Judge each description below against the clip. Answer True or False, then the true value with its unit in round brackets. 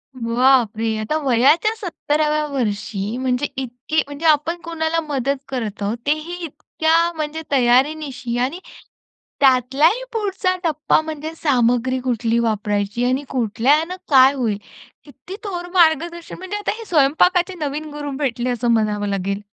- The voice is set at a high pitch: True (275 Hz)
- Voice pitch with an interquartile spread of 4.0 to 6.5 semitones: True (4.9 semitones)